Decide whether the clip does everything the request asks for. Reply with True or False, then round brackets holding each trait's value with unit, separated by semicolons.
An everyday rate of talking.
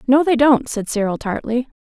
True (195 wpm)